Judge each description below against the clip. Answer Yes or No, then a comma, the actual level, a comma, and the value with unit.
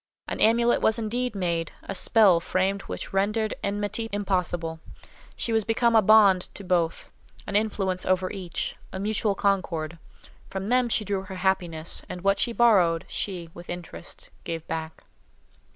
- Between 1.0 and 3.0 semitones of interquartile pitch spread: No, average, 3.5 semitones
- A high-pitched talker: Yes, high, 195 Hz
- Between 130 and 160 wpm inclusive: Yes, average, 155 wpm